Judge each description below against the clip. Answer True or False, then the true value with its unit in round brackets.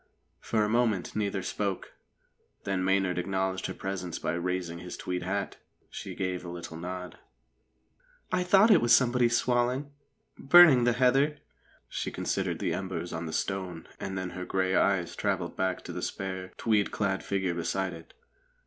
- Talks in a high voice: False (95 Hz)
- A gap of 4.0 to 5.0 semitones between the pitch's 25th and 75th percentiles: True (4.5 semitones)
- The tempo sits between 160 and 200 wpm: True (165 wpm)